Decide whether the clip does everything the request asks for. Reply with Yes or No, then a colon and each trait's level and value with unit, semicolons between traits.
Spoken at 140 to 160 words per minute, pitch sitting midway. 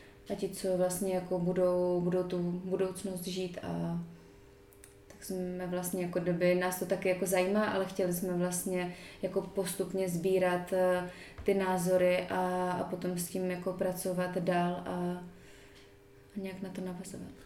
Yes: average, 150 wpm; medium, 180 Hz